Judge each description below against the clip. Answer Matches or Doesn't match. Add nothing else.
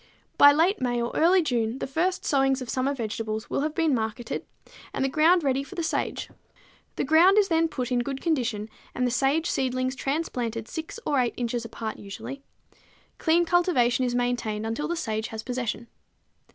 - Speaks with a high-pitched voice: Matches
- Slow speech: Doesn't match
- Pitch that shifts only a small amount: Doesn't match